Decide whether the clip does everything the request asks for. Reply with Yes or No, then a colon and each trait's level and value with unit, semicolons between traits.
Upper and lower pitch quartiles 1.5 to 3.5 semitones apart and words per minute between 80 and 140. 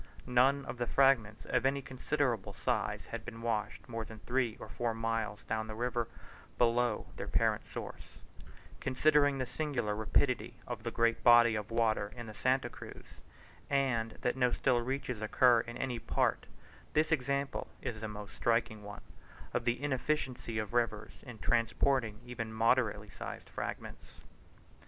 No: average, 2.8 semitones; average, 155 wpm